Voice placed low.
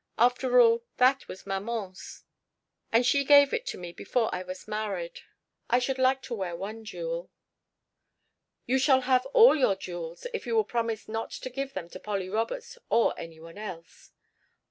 No: high, 230 Hz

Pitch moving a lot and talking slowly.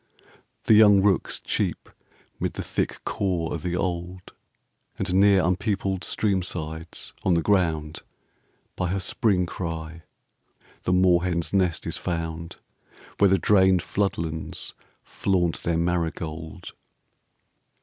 No: narrow, 2.6 semitones; slow, 120 wpm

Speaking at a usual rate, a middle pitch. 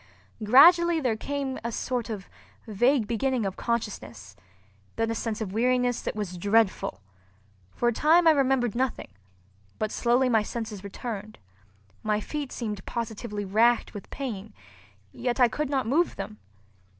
No: average, 150 wpm; high, 235 Hz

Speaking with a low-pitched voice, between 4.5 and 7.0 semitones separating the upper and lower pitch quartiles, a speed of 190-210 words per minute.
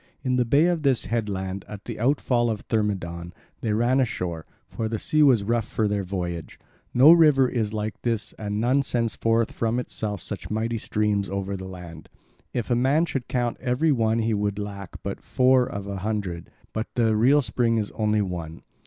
No: low, 110 Hz; average, 3.6 semitones; average, 195 wpm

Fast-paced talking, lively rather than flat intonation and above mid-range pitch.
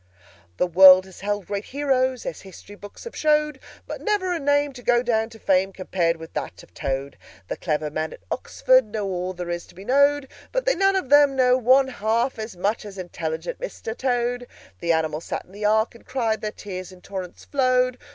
Yes: fast, 215 wpm; wide, 6.1 semitones; high, 220 Hz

